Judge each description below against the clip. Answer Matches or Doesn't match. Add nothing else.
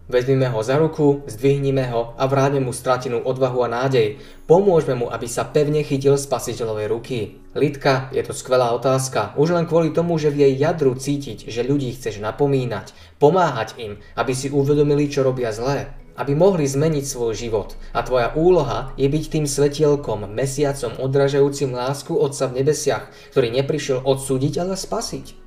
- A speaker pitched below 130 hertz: Doesn't match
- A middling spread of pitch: Doesn't match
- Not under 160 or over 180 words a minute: Matches